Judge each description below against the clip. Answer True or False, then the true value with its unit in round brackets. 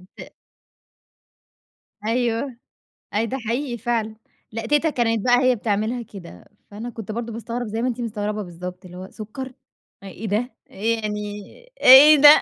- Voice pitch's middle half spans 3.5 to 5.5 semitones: False (2.8 semitones)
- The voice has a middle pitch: False (225 Hz)